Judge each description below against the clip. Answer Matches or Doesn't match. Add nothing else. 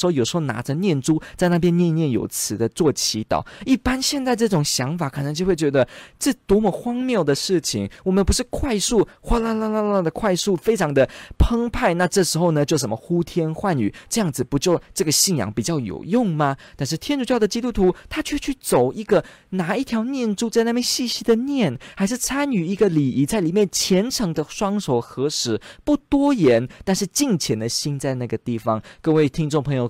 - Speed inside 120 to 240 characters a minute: Doesn't match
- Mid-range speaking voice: Matches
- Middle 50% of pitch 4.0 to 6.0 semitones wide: Doesn't match